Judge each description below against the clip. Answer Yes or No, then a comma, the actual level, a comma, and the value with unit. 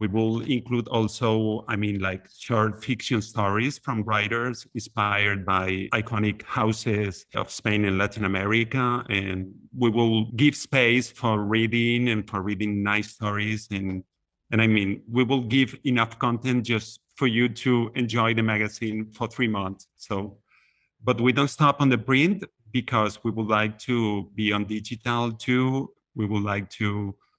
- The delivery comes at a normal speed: Yes, average, 160 wpm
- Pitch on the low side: Yes, low, 110 Hz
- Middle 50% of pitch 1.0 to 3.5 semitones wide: Yes, average, 2.7 semitones